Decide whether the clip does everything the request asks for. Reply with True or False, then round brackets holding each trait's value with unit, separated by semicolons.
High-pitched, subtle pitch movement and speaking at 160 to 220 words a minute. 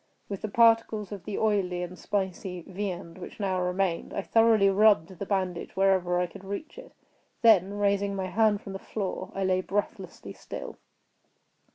True (195 Hz; 2.1 semitones; 170 wpm)